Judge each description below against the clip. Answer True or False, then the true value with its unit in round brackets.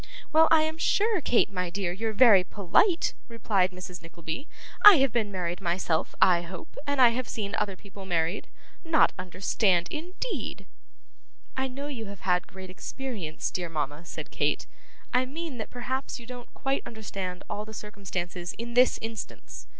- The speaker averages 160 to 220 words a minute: True (165 wpm)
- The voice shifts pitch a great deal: True (6.1 semitones)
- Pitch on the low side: False (210 Hz)